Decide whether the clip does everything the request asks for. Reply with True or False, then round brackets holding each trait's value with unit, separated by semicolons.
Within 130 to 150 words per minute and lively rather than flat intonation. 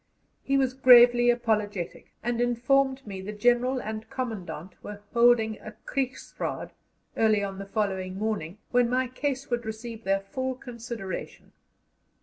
False (135 wpm; 3.2 semitones)